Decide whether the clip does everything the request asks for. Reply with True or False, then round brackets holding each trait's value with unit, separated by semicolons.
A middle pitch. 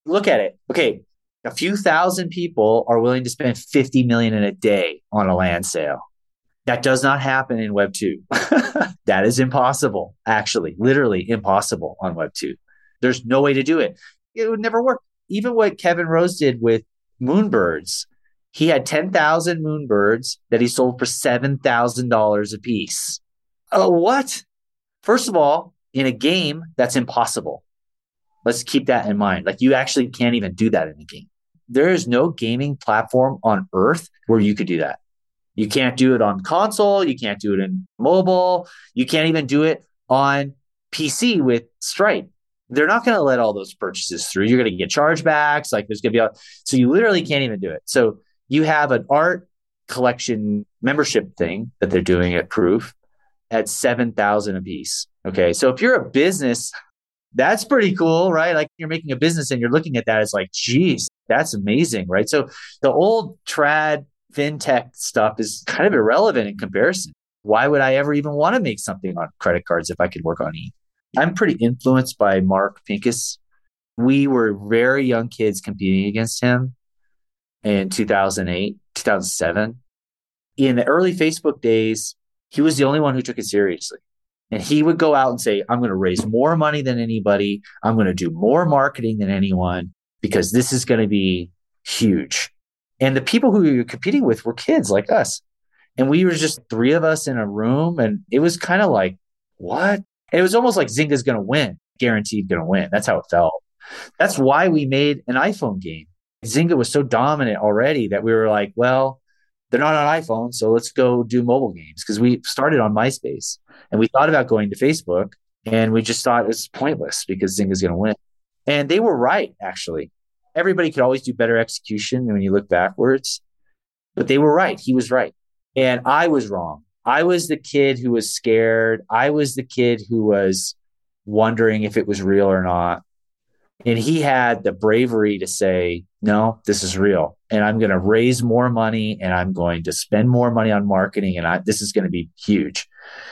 False (120 Hz)